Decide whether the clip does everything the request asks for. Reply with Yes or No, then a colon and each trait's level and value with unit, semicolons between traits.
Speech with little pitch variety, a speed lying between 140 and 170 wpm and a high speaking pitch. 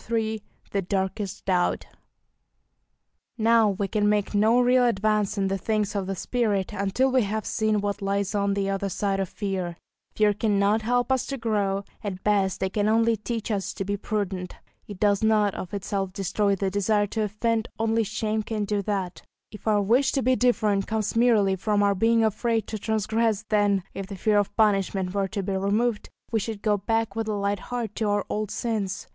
No: narrow, 2.0 semitones; average, 200 wpm; high, 210 Hz